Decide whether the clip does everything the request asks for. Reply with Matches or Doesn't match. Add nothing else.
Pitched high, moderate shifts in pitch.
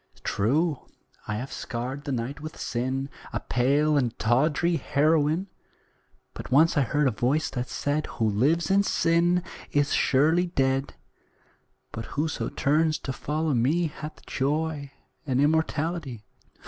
Doesn't match